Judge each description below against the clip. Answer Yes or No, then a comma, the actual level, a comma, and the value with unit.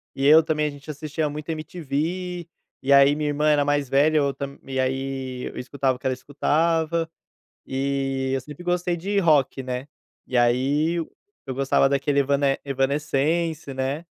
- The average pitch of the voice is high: No, medium, 145 Hz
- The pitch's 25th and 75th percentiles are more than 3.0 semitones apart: No, average, 2.7 semitones